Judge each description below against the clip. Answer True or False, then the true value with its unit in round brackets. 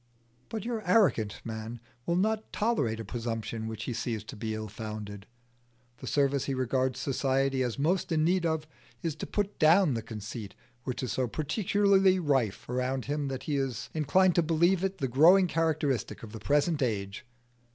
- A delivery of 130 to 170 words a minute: False (180 wpm)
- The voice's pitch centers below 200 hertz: True (135 Hz)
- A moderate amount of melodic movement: False (7.0 semitones)